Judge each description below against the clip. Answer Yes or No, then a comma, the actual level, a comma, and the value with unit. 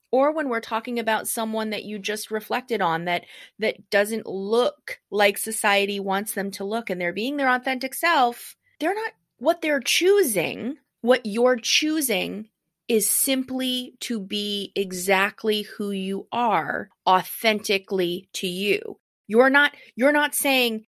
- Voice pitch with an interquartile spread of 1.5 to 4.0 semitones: No, average, 4.6 semitones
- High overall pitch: Yes, high, 225 Hz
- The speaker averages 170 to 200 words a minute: No, average, 145 wpm